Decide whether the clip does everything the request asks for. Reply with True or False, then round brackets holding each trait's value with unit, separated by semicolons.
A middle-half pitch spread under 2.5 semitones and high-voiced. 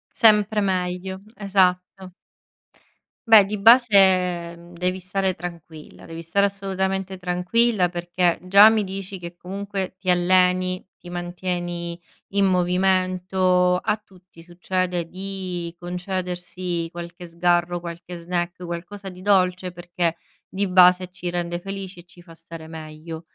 False (1.7 semitones; 180 Hz)